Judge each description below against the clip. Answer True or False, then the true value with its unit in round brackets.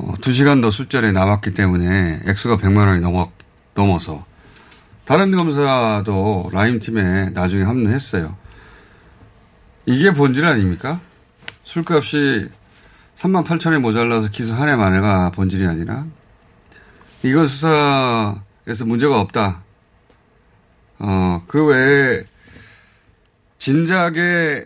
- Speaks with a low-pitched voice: True (110 Hz)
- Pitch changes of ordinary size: False (6.2 semitones)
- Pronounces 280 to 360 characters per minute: False (220 characters per minute)